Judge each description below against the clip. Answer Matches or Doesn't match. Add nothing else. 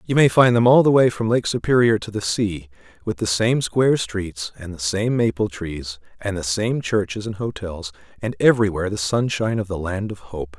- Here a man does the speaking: Matches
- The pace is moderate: Doesn't match